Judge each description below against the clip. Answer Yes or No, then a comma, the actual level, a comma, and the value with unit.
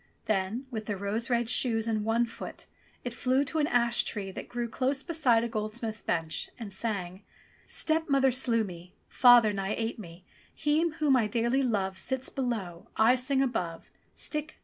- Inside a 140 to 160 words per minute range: No, average, 175 wpm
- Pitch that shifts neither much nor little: Yes, average, 3.8 semitones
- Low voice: No, high, 230 Hz